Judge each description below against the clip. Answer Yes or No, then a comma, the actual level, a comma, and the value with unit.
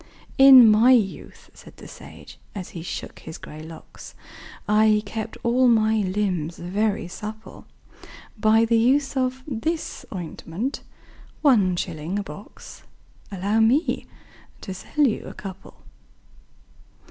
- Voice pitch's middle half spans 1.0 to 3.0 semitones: No, average, 4.4 semitones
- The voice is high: Yes, high, 215 Hz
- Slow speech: Yes, slow, 125 wpm